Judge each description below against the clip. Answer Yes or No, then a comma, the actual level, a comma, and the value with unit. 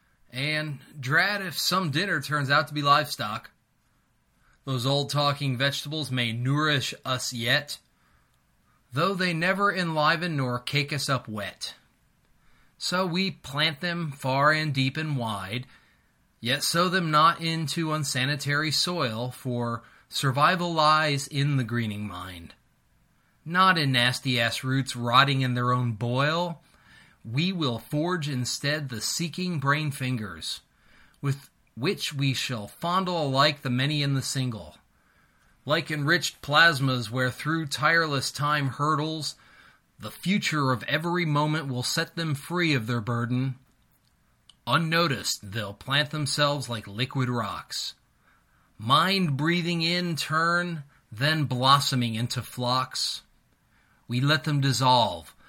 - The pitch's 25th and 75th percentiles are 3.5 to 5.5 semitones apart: Yes, average, 4.0 semitones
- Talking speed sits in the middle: No, slow, 125 wpm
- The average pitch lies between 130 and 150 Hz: Yes, medium, 140 Hz